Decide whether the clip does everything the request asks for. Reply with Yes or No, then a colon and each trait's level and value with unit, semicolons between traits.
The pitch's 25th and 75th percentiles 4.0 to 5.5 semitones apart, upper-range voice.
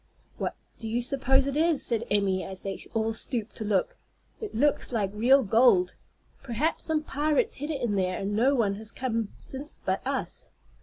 Yes: average, 4.9 semitones; high, 235 Hz